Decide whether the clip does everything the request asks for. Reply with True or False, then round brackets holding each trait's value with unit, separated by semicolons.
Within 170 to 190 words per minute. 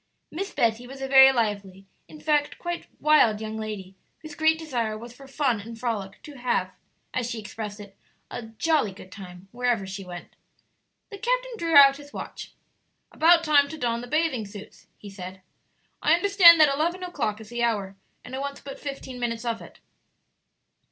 True (185 wpm)